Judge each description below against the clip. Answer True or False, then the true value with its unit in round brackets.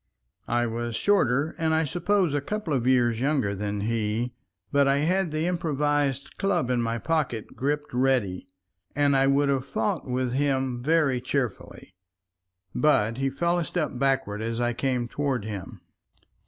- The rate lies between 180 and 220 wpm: False (160 wpm)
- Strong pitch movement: False (3.7 semitones)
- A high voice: False (135 Hz)